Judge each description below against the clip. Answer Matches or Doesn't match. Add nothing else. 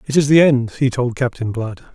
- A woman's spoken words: Doesn't match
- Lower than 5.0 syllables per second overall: Doesn't match